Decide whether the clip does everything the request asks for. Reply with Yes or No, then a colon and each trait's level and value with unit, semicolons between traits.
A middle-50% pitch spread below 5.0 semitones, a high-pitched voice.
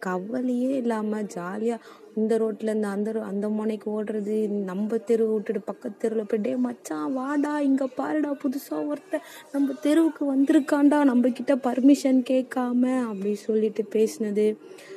Yes: average, 4.3 semitones; high, 240 Hz